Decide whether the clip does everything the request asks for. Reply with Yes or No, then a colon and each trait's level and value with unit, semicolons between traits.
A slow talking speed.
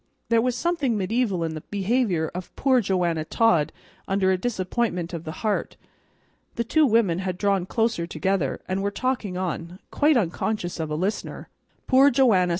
No: average, 165 wpm